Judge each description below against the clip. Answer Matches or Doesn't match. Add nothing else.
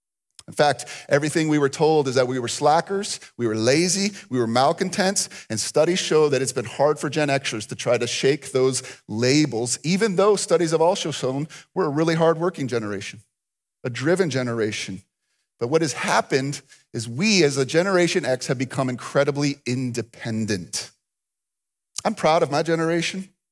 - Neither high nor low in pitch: Matches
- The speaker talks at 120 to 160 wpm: Doesn't match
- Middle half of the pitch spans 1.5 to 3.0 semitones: Doesn't match